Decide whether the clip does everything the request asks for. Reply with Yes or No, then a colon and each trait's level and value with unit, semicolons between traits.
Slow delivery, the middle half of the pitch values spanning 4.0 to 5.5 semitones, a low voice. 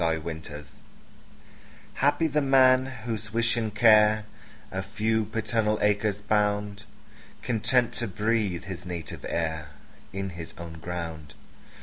Yes: slow, 125 wpm; average, 4.4 semitones; low, 105 Hz